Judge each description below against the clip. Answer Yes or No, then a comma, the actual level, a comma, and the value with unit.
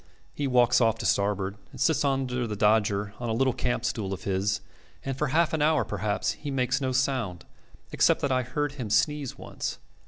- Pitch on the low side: Yes, low, 125 Hz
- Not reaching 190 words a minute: No, average, 195 wpm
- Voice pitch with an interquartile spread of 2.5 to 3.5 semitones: No, average, 4.5 semitones